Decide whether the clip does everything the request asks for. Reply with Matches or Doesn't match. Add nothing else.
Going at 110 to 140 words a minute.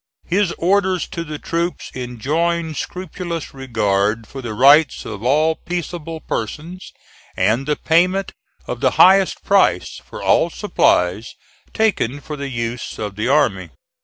Matches